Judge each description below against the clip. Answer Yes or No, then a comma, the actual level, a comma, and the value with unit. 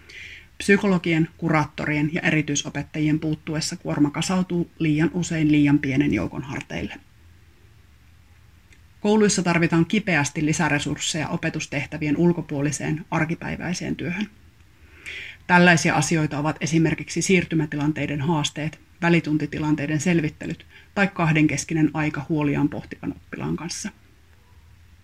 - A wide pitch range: No, average, 2.8 semitones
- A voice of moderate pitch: Yes, medium, 155 Hz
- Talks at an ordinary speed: No, slow, 85 wpm